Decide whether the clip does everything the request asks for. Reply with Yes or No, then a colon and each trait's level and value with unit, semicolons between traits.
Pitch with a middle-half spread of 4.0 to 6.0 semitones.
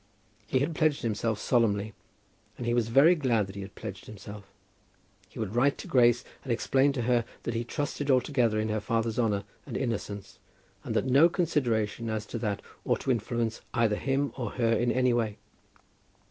No: average, 3.3 semitones